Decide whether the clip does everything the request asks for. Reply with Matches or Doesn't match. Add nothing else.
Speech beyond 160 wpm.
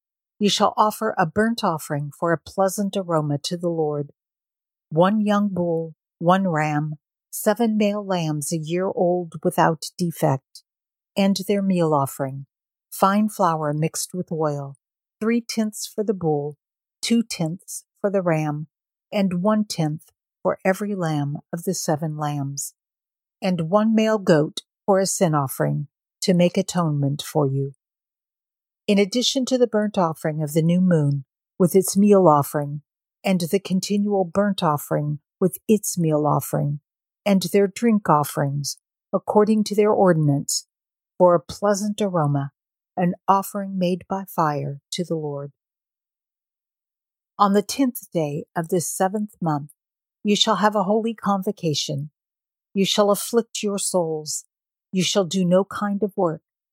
Doesn't match